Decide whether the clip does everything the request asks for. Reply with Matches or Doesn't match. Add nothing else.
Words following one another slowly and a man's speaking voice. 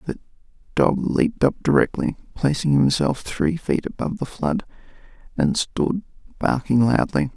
Matches